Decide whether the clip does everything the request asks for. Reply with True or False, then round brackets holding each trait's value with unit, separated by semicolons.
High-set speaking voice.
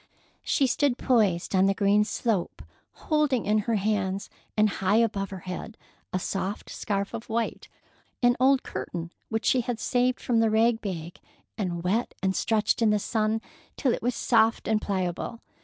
True (215 Hz)